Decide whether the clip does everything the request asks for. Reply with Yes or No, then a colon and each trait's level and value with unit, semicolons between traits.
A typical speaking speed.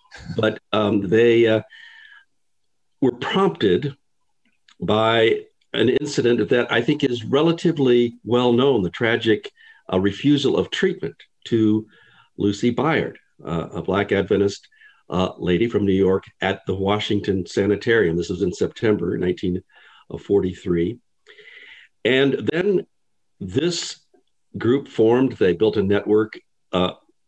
No: slow, 115 wpm